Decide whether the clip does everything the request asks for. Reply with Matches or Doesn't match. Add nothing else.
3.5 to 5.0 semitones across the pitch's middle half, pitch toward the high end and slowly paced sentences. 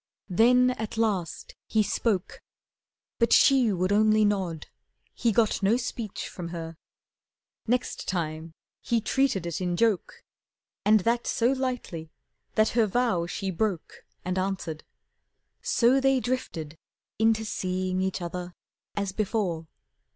Matches